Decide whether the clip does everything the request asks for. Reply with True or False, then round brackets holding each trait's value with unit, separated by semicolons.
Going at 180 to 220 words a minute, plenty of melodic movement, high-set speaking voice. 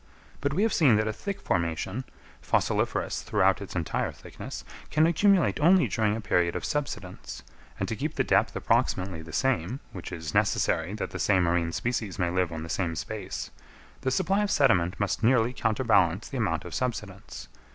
False (185 wpm; 7.2 semitones; 105 Hz)